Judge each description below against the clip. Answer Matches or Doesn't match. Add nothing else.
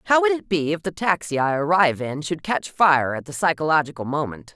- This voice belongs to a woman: Matches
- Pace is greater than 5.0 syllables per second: Matches